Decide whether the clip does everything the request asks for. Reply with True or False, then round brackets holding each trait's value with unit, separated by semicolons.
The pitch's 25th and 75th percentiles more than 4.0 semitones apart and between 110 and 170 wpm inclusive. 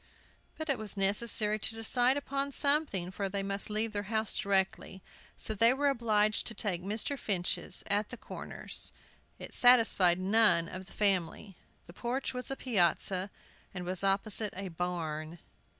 False (3.5 semitones; 160 wpm)